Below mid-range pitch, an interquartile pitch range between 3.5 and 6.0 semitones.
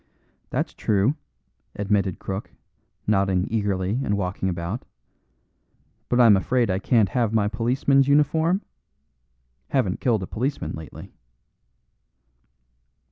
Yes: low, 105 Hz; average, 4.6 semitones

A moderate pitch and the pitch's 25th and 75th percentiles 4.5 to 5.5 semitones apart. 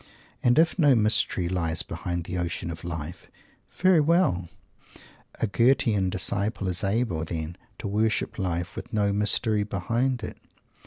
No: low, 100 Hz; average, 4.9 semitones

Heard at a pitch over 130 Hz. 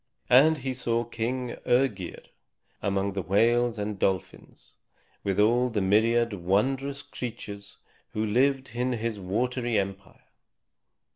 No: low, 115 Hz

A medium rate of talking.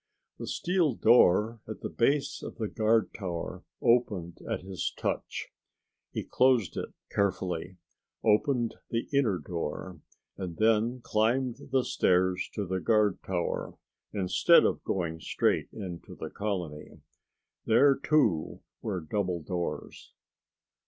No: slow, 125 wpm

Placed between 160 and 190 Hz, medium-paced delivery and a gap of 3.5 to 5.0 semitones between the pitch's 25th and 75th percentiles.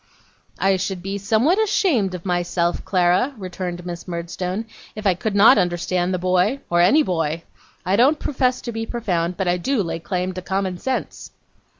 Yes: medium, 185 Hz; average, 180 wpm; average, 3.8 semitones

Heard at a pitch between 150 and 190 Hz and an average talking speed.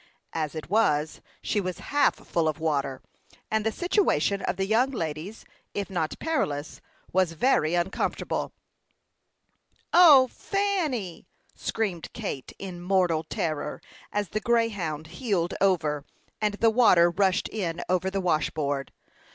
No: medium, 185 Hz; slow, 130 wpm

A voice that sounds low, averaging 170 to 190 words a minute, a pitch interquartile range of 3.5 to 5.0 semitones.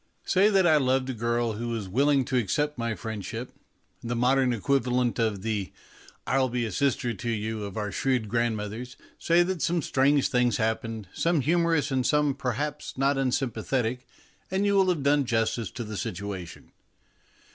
Yes: low, 125 Hz; average, 180 wpm; average, 4.0 semitones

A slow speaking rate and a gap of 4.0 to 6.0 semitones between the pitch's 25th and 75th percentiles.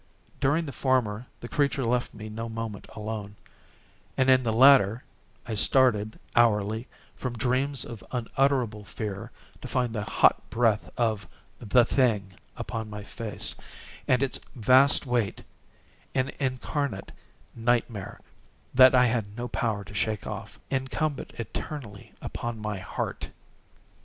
No: slow, 125 wpm; average, 3.3 semitones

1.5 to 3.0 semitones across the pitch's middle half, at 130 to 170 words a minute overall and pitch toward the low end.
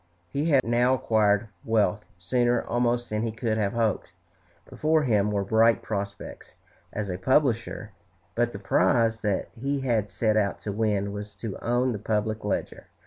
Yes: average, 2.7 semitones; average, 165 wpm; low, 110 Hz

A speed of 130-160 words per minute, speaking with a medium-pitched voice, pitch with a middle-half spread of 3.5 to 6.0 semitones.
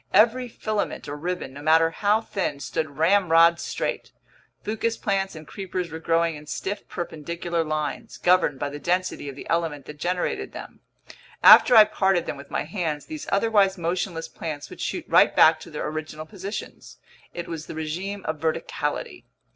No: average, 170 wpm; medium, 170 Hz; average, 3.8 semitones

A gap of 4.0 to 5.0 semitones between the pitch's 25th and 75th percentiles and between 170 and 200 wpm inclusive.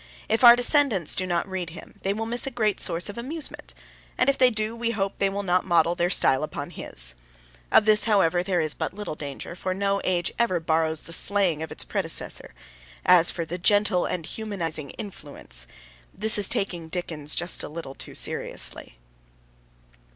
Yes: average, 4.3 semitones; average, 190 wpm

